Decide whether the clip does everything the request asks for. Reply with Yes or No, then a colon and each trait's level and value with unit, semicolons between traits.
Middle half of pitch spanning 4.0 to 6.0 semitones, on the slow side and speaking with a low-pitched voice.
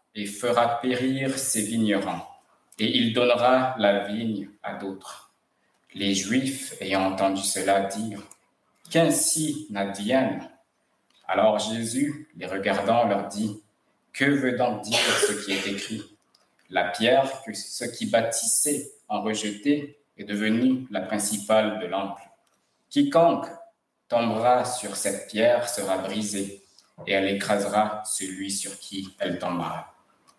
Yes: average, 4.3 semitones; slow, 125 wpm; low, 110 Hz